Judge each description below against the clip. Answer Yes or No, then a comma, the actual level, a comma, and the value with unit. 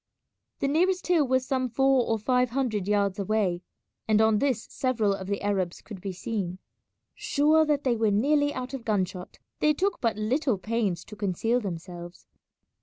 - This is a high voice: Yes, high, 225 Hz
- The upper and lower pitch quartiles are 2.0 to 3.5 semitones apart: No, average, 5.1 semitones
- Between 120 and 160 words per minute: No, average, 180 wpm